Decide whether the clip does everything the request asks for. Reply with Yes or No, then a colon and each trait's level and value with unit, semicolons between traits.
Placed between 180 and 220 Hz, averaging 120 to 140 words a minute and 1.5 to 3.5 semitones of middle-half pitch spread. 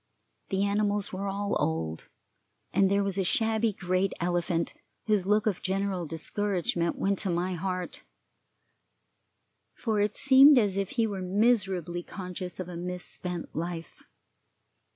Yes: high, 190 Hz; slow, 135 wpm; narrow, 2.5 semitones